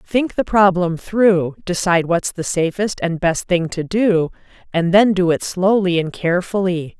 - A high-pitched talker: No, medium, 180 Hz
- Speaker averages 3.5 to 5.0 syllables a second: Yes, 4.4 syllables/s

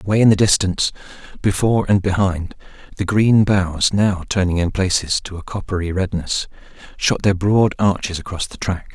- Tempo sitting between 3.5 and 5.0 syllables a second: No, 5.2 syllables/s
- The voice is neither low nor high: No, very low, 95 Hz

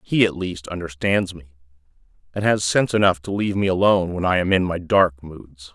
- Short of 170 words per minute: No, average, 200 wpm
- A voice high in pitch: No, very low, 90 Hz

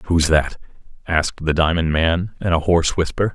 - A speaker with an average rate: Yes, average, 180 wpm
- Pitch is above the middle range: No, very low, 85 Hz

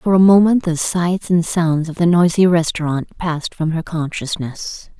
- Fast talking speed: No, average, 180 wpm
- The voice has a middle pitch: Yes, medium, 170 Hz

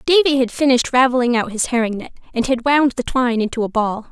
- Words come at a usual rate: No, fast, 235 wpm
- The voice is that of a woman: Yes, female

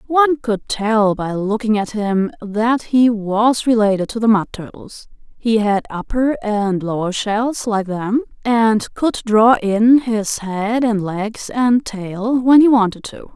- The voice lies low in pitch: No, high, 220 Hz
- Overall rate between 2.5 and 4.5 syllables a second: Yes, 3.7 syllables/s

